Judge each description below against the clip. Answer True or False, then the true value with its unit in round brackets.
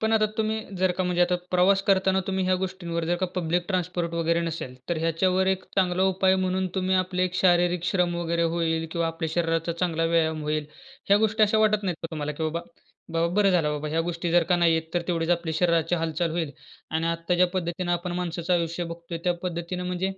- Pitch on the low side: False (175 Hz)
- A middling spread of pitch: False (1.9 semitones)